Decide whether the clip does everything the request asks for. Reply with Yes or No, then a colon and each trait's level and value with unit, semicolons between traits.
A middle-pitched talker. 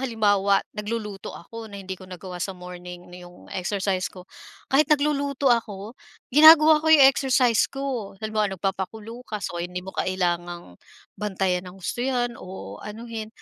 No: high, 205 Hz